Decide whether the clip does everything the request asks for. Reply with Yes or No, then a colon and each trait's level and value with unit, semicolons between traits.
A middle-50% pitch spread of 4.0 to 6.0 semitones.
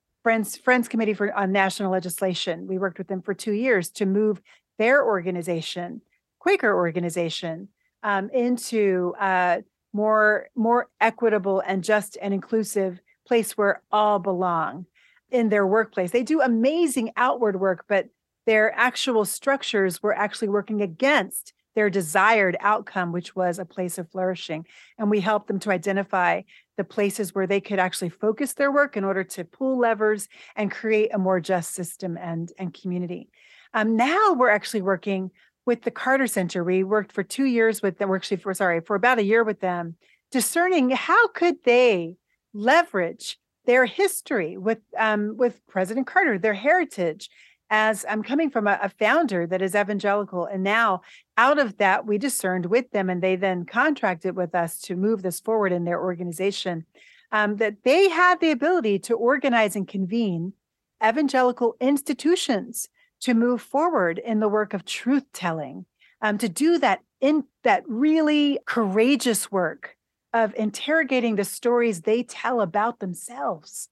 Yes: average, 4.3 semitones